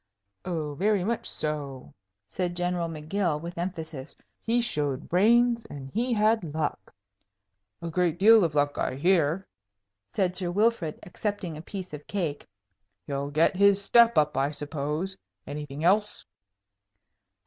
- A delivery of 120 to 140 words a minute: Yes, slow, 135 wpm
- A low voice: No, medium, 170 Hz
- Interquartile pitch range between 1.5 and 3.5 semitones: No, average, 5.1 semitones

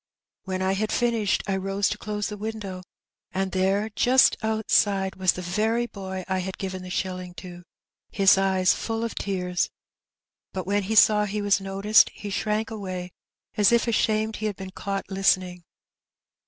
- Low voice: No, high, 195 Hz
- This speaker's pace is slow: No, average, 175 wpm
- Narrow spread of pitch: Yes, narrow, 2.3 semitones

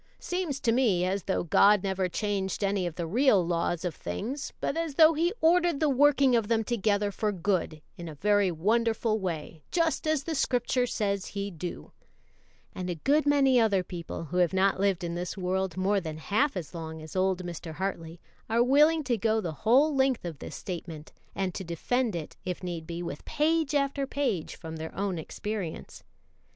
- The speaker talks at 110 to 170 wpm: No, average, 195 wpm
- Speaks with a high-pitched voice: Yes, high, 200 Hz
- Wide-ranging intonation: Yes, wide, 6.9 semitones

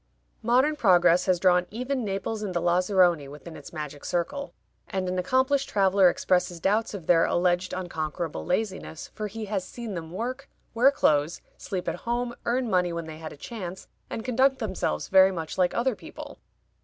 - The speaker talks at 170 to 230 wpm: Yes, average, 180 wpm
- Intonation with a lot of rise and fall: No, average, 4.8 semitones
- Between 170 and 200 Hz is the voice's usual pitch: Yes, high, 190 Hz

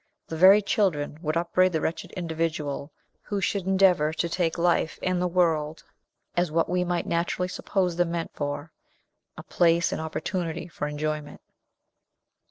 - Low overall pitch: No, medium, 170 Hz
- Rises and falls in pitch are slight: Yes, narrow, 2.3 semitones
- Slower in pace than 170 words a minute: Yes, average, 160 wpm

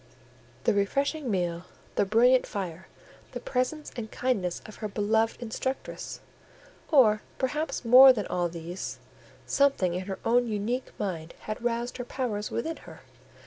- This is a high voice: Yes, high, 225 Hz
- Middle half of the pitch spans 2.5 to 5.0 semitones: Yes, average, 4.5 semitones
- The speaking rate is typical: Yes, average, 145 wpm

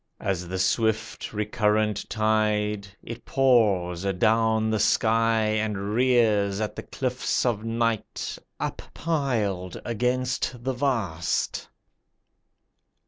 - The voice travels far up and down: No, narrow, 2.5 semitones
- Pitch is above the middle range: No, low, 110 Hz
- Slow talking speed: Yes, slow, 95 wpm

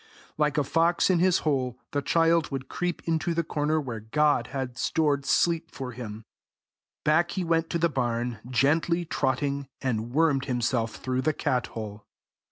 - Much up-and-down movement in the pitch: No, average, 4.6 semitones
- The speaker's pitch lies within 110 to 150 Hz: Yes, medium, 140 Hz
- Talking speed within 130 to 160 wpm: No, average, 170 wpm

